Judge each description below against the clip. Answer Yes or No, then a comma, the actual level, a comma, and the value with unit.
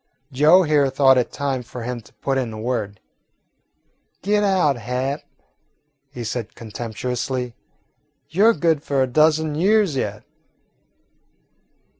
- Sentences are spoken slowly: Yes, slow, 130 wpm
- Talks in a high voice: No, low, 135 Hz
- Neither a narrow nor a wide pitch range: Yes, average, 4.2 semitones